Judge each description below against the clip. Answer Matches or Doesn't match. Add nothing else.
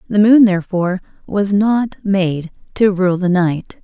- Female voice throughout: Matches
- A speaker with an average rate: Matches